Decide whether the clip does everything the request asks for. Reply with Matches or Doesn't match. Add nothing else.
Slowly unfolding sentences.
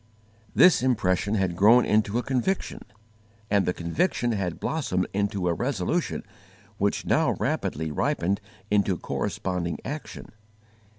Matches